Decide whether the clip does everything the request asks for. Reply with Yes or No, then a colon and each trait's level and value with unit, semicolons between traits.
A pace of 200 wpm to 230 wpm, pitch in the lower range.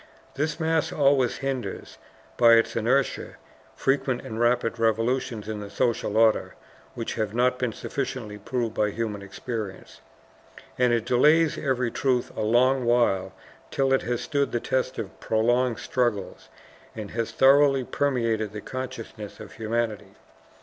No: average, 145 wpm; low, 120 Hz